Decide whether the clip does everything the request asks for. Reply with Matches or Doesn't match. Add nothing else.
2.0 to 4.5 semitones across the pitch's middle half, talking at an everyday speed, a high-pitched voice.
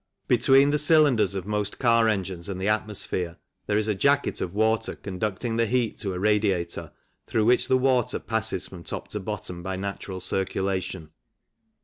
Doesn't match